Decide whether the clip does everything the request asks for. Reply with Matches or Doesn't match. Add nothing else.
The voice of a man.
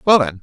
Matches